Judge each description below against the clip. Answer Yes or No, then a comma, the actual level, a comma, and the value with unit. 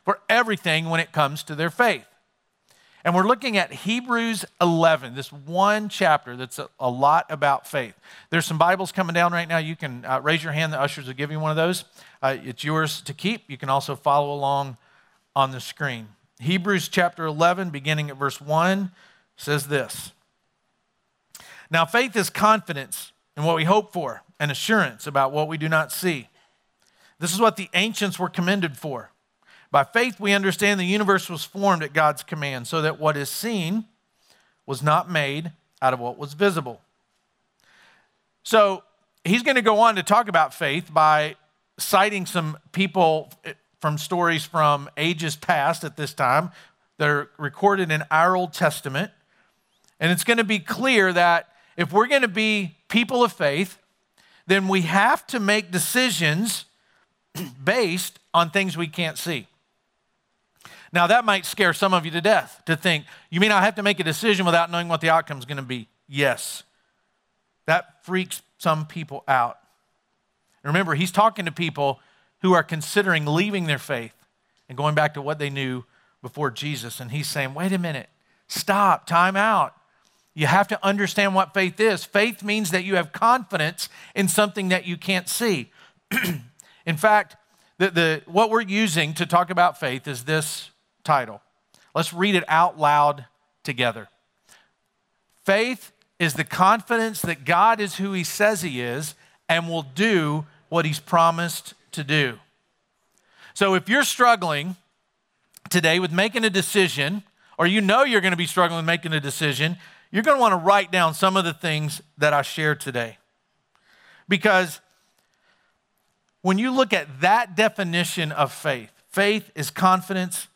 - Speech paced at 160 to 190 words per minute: Yes, average, 170 wpm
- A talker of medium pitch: Yes, medium, 170 Hz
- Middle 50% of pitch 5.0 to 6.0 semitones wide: No, average, 4.6 semitones